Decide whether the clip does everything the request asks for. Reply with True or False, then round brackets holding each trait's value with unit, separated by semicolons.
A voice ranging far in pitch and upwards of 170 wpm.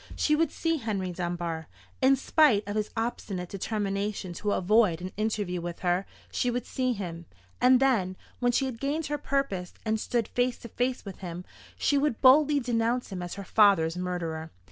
True (5.7 semitones; 185 wpm)